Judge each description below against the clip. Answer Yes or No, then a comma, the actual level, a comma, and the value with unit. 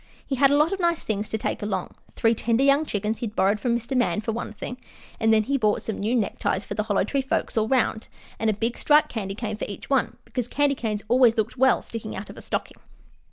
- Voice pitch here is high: Yes, high, 225 Hz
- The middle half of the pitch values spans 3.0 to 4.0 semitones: Yes, average, 3.7 semitones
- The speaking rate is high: Yes, fast, 250 wpm